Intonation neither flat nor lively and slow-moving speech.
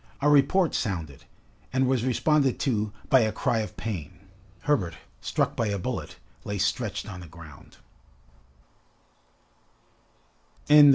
No: wide, 6.1 semitones; slow, 120 wpm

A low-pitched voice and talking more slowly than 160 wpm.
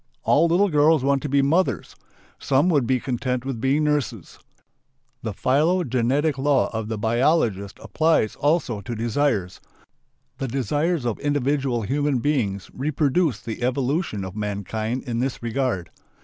Yes: low, 130 Hz; average, 140 wpm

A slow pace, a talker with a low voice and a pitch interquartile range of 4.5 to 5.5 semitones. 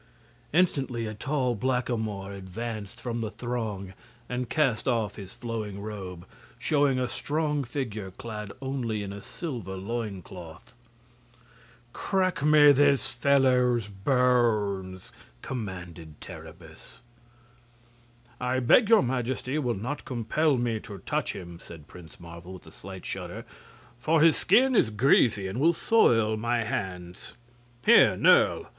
Yes: slow, 125 wpm; low, 115 Hz; average, 5.1 semitones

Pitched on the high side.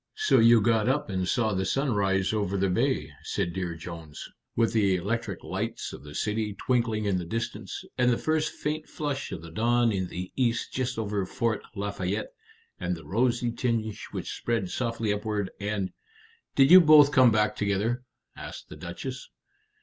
No: low, 110 Hz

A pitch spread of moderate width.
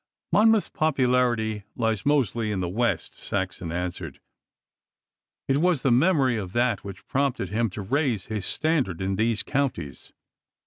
No: wide, 5.9 semitones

